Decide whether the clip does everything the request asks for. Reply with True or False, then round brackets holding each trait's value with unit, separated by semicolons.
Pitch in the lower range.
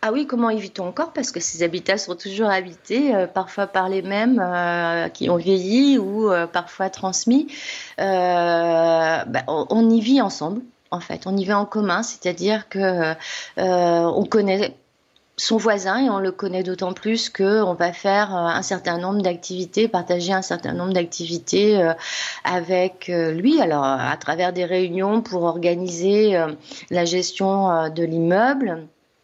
False (185 Hz)